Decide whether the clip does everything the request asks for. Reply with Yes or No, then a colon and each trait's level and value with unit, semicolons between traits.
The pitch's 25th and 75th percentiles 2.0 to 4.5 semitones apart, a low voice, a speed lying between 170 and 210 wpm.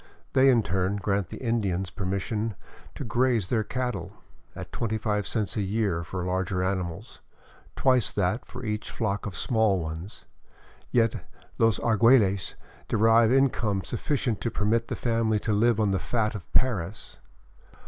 No: average, 3.2 semitones; low, 105 Hz; average, 155 wpm